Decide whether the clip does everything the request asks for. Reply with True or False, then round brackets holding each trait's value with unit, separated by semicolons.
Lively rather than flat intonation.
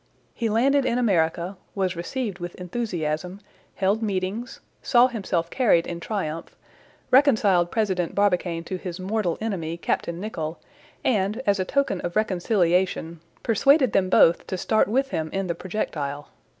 False (4.3 semitones)